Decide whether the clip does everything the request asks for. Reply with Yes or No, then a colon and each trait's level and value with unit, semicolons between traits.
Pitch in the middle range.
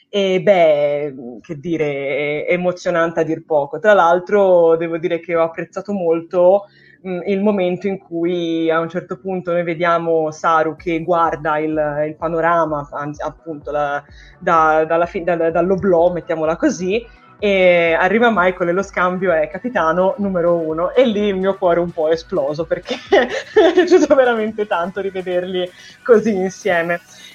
Yes: medium, 175 Hz